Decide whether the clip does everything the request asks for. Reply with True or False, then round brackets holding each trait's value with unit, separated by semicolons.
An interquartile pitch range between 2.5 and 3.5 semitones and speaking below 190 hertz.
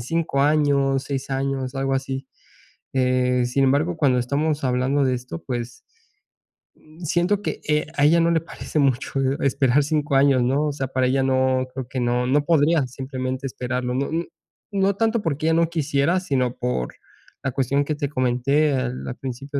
True (2.8 semitones; 135 Hz)